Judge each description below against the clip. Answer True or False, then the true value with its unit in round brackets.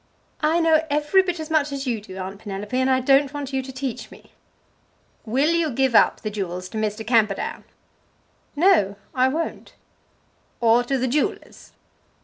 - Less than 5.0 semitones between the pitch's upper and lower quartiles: False (5.4 semitones)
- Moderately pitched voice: False (260 Hz)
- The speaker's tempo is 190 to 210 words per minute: False (170 wpm)